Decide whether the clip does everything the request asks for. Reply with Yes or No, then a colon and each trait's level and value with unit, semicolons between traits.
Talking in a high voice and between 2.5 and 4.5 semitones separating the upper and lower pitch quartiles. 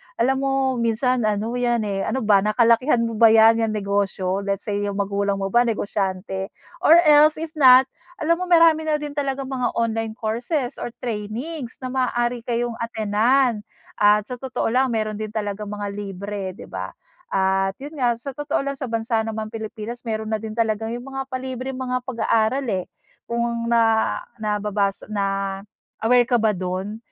Yes: high, 225 Hz; average, 3.6 semitones